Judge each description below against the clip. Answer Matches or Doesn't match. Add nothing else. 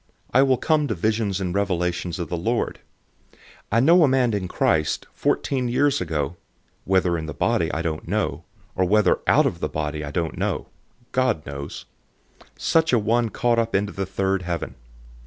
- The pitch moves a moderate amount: Doesn't match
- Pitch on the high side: Doesn't match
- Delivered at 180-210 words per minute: Matches